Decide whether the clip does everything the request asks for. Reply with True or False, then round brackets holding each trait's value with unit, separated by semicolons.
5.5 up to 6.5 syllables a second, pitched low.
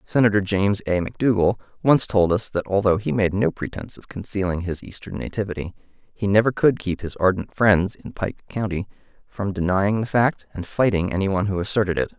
True (5.7 syllables/s; 100 Hz)